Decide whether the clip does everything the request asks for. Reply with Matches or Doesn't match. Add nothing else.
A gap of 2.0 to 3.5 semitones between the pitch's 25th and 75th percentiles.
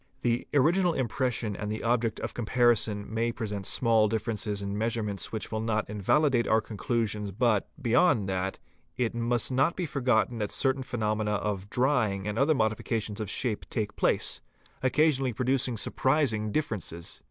Matches